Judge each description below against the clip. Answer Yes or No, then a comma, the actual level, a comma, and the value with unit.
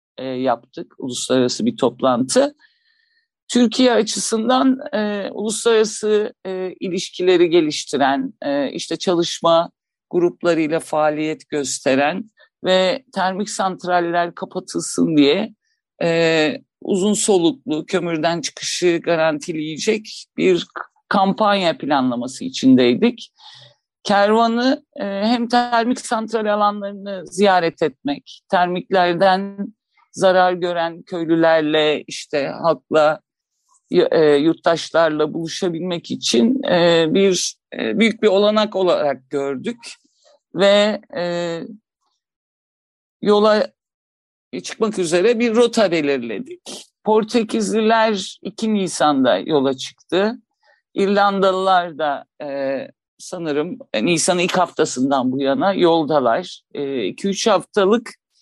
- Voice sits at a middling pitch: No, high, 195 Hz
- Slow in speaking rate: Yes, slow, 80 wpm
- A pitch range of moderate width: No, wide, 5.8 semitones